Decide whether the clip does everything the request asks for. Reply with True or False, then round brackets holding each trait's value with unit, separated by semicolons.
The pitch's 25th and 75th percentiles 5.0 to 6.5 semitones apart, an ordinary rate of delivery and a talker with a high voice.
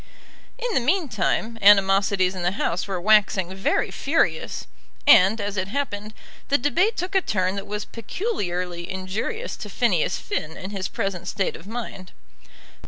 True (5.6 semitones; 155 wpm; 200 Hz)